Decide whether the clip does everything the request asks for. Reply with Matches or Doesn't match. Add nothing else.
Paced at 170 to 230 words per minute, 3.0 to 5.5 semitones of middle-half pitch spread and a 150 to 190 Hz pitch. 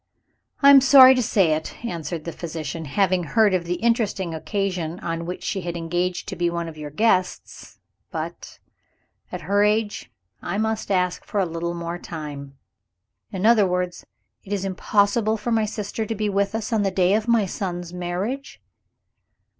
Matches